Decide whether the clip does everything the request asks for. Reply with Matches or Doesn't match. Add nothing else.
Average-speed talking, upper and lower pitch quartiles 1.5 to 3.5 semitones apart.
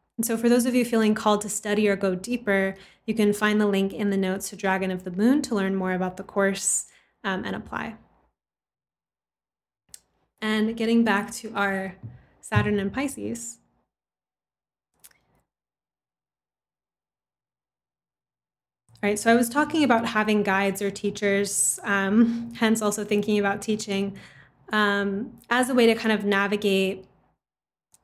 Matches